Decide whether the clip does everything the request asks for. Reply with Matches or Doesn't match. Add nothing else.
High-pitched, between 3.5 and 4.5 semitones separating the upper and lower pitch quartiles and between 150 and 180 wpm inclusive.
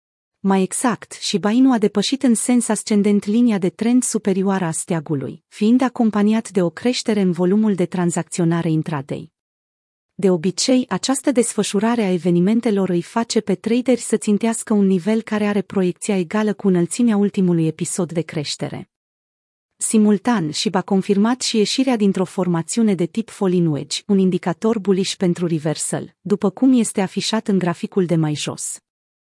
Matches